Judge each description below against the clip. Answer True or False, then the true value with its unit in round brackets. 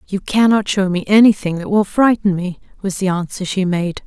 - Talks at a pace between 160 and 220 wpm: True (205 wpm)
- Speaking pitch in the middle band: False (195 Hz)